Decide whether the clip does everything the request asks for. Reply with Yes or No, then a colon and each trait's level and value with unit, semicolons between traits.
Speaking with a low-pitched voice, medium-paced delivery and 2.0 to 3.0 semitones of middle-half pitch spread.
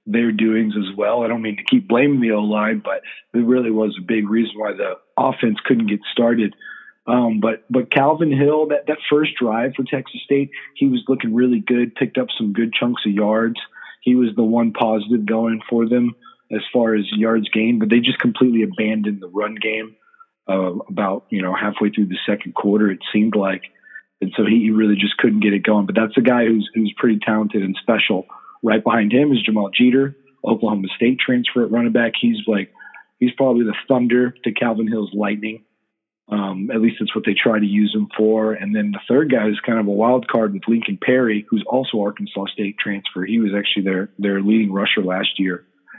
No: low, 110 Hz; fast, 215 wpm; narrow, 2.5 semitones